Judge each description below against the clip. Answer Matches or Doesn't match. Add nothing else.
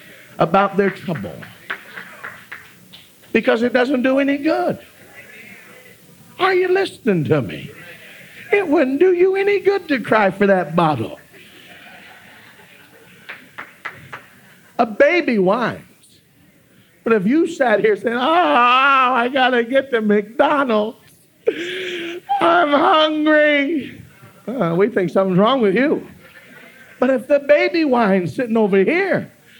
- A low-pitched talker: Doesn't match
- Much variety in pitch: Matches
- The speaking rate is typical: Doesn't match